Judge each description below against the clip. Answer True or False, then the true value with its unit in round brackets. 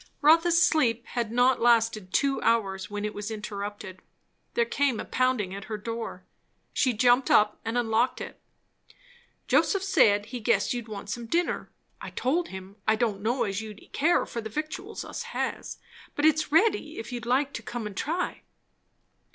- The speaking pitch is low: False (235 Hz)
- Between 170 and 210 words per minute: True (175 wpm)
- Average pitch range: True (4.7 semitones)